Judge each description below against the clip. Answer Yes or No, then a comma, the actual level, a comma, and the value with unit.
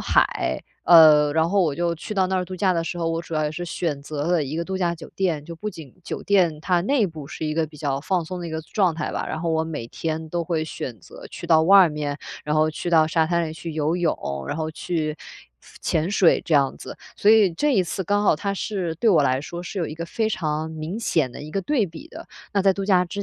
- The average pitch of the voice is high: No, medium, 165 Hz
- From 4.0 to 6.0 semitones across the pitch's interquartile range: No, average, 2.8 semitones